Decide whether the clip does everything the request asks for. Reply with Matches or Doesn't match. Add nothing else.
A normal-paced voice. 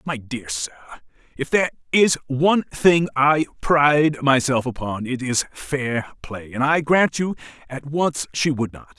Matches